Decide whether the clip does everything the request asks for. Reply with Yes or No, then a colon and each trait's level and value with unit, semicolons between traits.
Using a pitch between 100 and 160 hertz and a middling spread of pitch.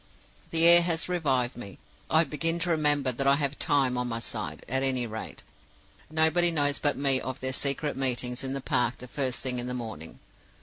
Yes: low, 135 Hz; average, 3.5 semitones